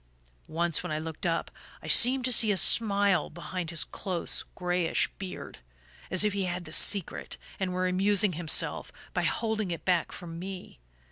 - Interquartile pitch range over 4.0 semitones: No, average, 2.9 semitones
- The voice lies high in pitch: No, medium, 180 Hz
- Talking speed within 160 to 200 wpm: Yes, average, 175 wpm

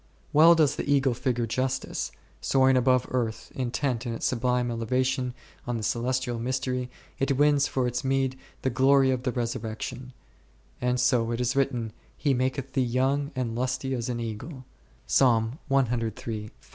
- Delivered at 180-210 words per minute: No, average, 155 wpm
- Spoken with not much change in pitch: Yes, narrow, 2.0 semitones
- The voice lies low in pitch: Yes, low, 125 Hz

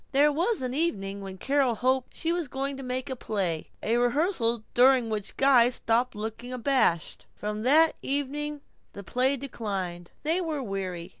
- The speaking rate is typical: Yes, average, 165 wpm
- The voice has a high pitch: Yes, very high, 250 Hz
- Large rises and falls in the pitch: No, average, 4.9 semitones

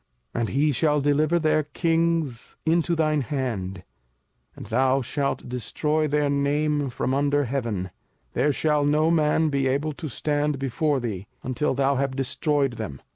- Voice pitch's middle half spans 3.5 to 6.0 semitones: No, average, 2.7 semitones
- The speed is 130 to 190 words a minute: Yes, average, 155 wpm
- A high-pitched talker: No, medium, 145 Hz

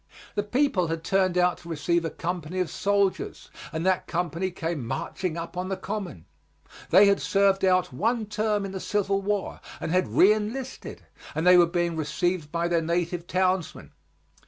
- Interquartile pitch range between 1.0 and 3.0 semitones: Yes, average, 2.7 semitones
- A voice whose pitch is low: No, medium, 180 Hz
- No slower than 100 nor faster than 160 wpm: No, average, 175 wpm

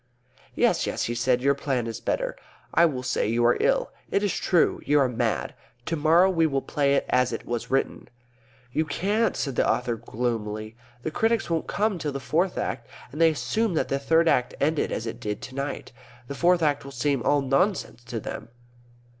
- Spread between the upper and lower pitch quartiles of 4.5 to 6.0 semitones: Yes, average, 5.1 semitones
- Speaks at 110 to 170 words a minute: No, fast, 205 wpm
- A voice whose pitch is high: No, medium, 140 Hz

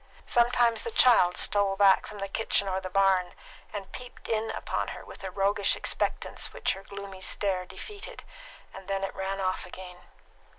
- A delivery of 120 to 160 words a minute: No, average, 175 wpm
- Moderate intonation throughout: No, narrow, 1.9 semitones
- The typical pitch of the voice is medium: No, high, 195 Hz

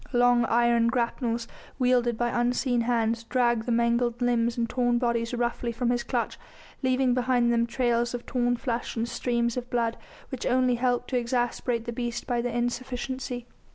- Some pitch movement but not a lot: No, narrow, 0.8 semitones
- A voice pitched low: No, high, 240 Hz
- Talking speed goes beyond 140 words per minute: Yes, average, 170 wpm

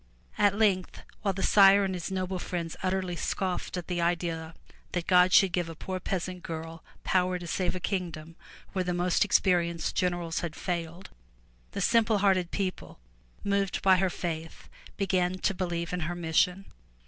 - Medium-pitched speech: Yes, medium, 180 Hz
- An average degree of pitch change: No, narrow, 1.9 semitones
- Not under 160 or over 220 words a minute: Yes, average, 170 wpm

